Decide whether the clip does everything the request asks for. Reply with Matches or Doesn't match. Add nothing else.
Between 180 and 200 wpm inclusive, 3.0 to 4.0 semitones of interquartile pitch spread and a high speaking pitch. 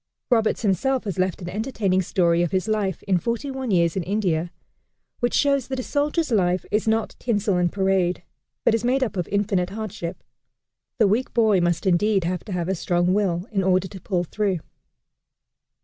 Matches